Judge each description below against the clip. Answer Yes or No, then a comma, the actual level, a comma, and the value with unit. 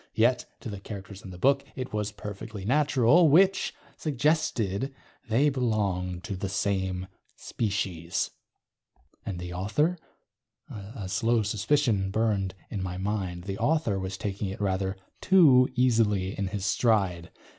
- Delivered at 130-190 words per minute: Yes, slow, 135 wpm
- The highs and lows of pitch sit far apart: No, average, 4.7 semitones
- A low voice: Yes, low, 105 Hz